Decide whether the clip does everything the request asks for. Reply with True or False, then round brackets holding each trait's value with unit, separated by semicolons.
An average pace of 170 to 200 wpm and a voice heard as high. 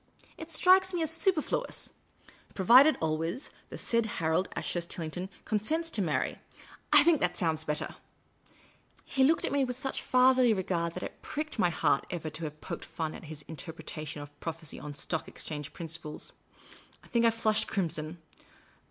False (180 wpm; 175 Hz)